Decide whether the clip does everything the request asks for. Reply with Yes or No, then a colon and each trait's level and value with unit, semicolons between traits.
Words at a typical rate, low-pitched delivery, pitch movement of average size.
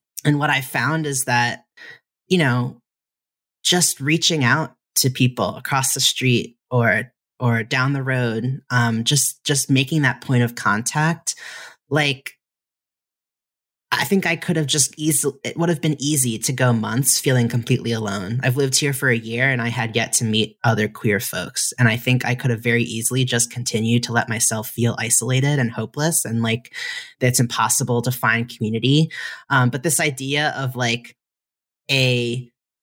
Yes: average, 170 wpm; low, 125 Hz; average, 3.5 semitones